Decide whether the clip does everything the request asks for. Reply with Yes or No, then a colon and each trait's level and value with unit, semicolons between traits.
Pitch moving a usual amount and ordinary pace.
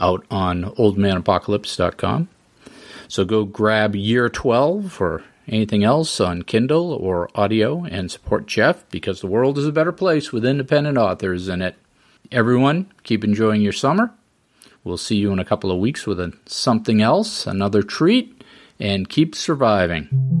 No: wide, 6.7 semitones; average, 155 wpm